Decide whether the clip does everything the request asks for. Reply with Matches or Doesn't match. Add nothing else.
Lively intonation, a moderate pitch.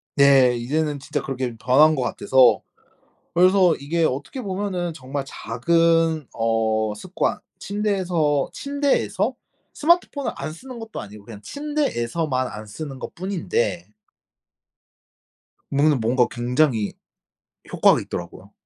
Matches